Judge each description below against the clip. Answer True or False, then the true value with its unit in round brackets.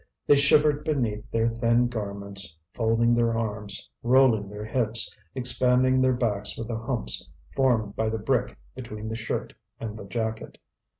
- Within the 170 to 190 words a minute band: False (155 wpm)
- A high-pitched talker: False (115 Hz)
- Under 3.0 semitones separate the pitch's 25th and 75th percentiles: True (2.6 semitones)